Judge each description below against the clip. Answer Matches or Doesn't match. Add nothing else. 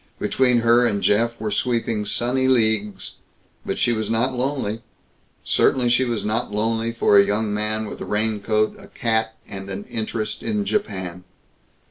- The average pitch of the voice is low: Matches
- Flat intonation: Matches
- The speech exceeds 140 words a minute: Matches